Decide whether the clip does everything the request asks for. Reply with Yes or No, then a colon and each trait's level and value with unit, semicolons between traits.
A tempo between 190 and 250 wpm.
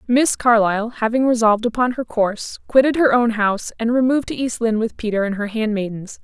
Yes: average, 200 wpm